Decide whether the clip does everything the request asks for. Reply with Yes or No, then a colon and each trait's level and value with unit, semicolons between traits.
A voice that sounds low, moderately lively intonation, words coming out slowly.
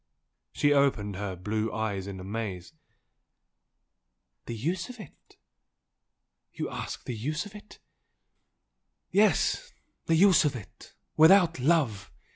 No: low, 130 Hz; wide, 8.6 semitones; slow, 125 wpm